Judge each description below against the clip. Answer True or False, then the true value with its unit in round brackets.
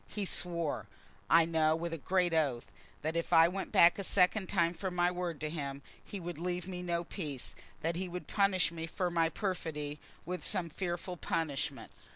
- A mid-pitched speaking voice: True (170 Hz)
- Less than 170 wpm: False (195 wpm)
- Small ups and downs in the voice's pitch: True (1.9 semitones)